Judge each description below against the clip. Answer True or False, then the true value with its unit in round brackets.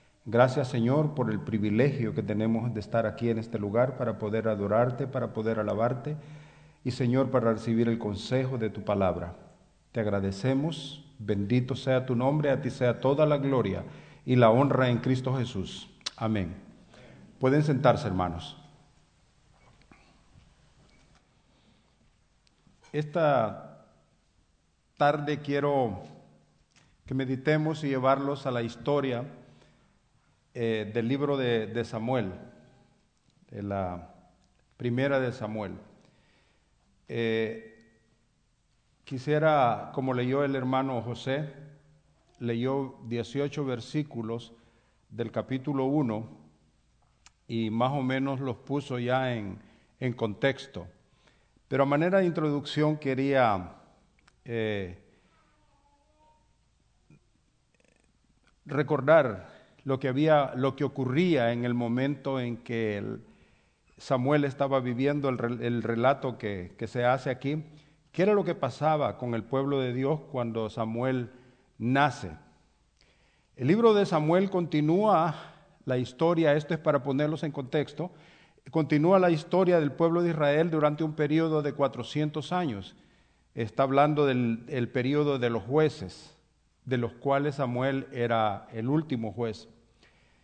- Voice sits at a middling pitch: False (130 Hz)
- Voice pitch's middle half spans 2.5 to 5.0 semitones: True (4.1 semitones)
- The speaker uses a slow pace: True (115 wpm)